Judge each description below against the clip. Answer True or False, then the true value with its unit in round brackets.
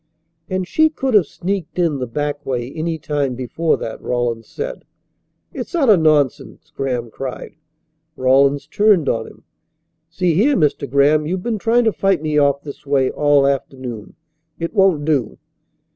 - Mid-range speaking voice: True (150 Hz)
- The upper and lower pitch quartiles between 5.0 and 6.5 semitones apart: True (5.6 semitones)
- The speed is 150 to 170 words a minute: True (160 wpm)